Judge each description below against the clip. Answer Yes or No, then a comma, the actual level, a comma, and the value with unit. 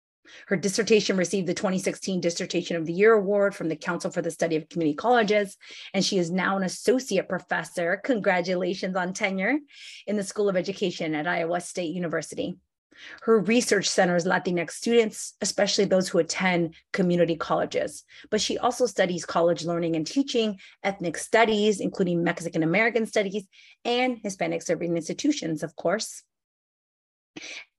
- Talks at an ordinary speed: Yes, average, 150 wpm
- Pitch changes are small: No, average, 3.8 semitones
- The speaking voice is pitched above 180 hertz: Yes, high, 190 Hz